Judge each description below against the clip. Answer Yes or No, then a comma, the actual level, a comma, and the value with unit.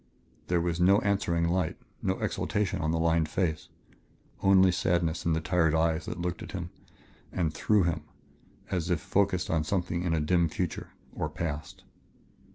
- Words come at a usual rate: Yes, average, 165 wpm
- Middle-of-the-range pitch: No, very low, 85 Hz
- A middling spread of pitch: No, narrow, 2.0 semitones